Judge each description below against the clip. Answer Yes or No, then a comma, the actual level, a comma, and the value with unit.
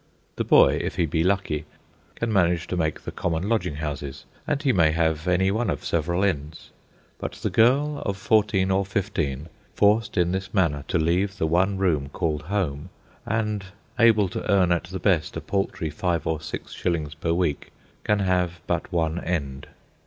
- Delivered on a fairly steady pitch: No, average, 3.8 semitones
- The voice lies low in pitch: Yes, very low, 90 Hz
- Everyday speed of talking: Yes, average, 180 wpm